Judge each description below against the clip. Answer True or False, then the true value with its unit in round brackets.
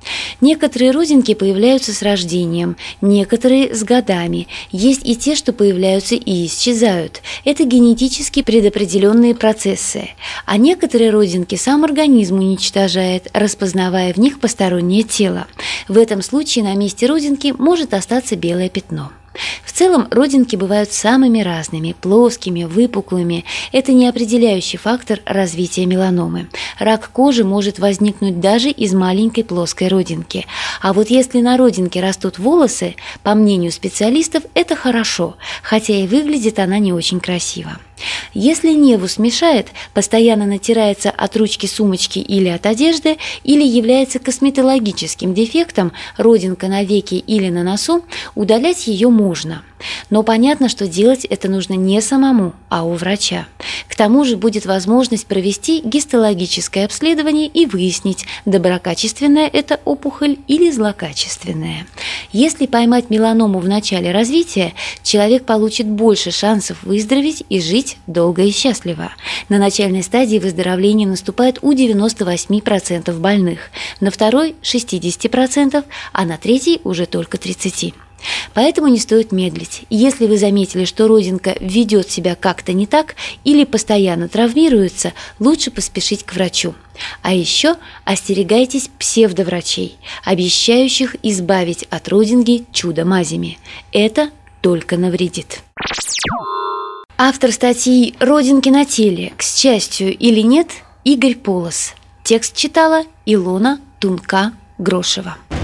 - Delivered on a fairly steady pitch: False (5.2 semitones)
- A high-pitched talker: True (210 Hz)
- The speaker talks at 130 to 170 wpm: False (120 wpm)